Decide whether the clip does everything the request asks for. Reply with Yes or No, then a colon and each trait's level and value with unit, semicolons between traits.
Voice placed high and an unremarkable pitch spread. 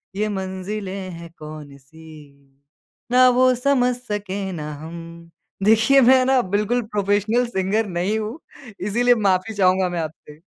Yes: high, 200 Hz; average, 5.0 semitones